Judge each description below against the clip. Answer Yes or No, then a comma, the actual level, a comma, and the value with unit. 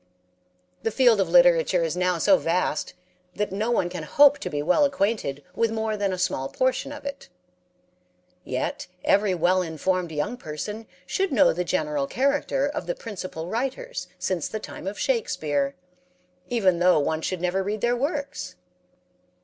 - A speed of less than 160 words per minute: No, average, 165 wpm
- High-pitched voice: Yes, high, 195 Hz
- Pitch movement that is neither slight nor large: No, wide, 6.2 semitones